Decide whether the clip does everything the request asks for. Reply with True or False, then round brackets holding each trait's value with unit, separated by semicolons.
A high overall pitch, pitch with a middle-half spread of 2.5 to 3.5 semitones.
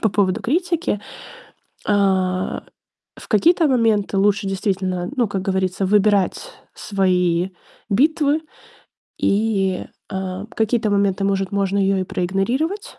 True (200 Hz; 2.9 semitones)